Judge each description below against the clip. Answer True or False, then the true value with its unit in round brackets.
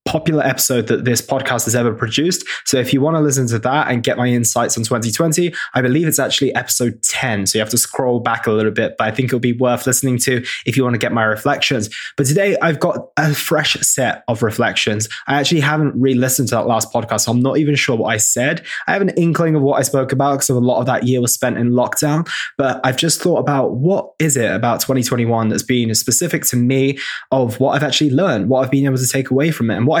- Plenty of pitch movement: False (2.8 semitones)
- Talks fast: True (260 wpm)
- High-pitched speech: False (130 Hz)